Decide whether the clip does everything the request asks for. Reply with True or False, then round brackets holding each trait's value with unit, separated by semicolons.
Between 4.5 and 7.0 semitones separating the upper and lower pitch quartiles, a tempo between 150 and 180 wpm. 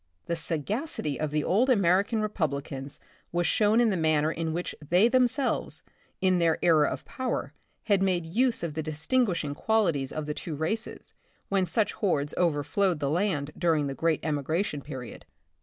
True (5.3 semitones; 170 wpm)